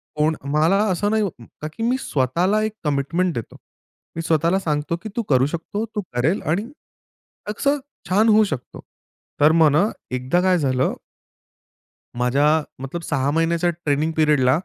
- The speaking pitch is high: No, medium, 160 Hz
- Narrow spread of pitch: No, average, 5.0 semitones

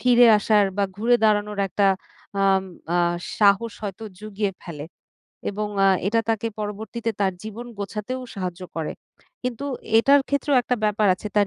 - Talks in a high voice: Yes, high, 210 Hz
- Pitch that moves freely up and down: No, narrow, 2.5 semitones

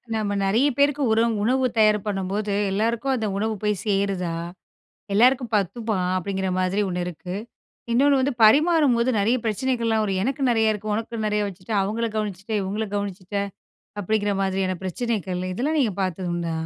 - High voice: Yes, high, 215 Hz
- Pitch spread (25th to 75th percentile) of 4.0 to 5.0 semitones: No, average, 3.4 semitones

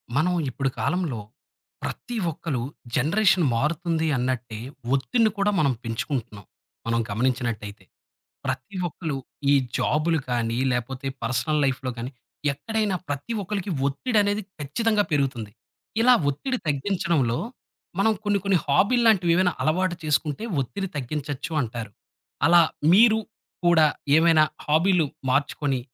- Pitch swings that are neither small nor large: No, wide, 6.5 semitones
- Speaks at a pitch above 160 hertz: No, medium, 150 Hz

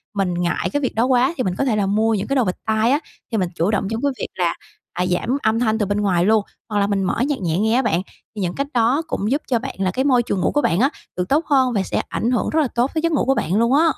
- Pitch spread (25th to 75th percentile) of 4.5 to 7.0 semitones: Yes, average, 5.1 semitones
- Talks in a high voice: Yes, high, 220 Hz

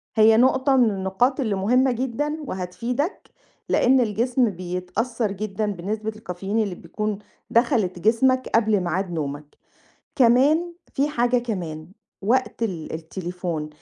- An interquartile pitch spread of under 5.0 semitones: No, wide, 5.4 semitones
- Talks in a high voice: Yes, high, 215 Hz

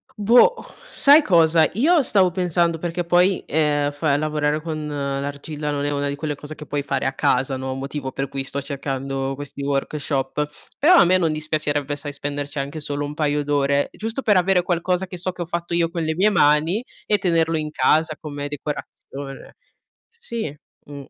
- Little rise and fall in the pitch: No, average, 3.4 semitones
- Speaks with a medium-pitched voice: Yes, medium, 150 Hz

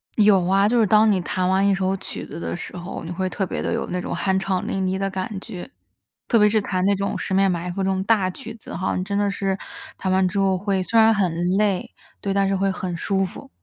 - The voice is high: Yes, high, 195 Hz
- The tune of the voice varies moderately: No, narrow, 1.3 semitones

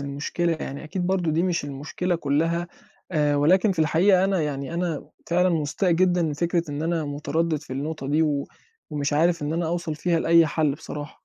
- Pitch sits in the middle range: Yes, medium, 160 Hz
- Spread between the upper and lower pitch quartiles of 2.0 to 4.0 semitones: Yes, average, 2.9 semitones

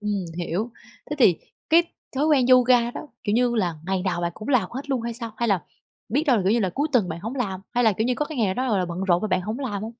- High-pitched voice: Yes, high, 225 Hz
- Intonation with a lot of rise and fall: No, average, 5.0 semitones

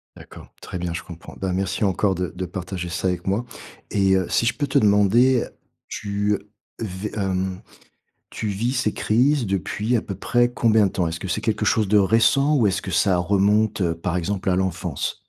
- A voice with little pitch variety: No, average, 3.0 semitones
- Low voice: Yes, low, 100 Hz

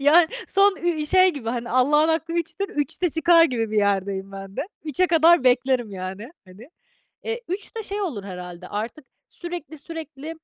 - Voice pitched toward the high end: Yes, very high, 295 Hz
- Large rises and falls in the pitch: Yes, wide, 8.0 semitones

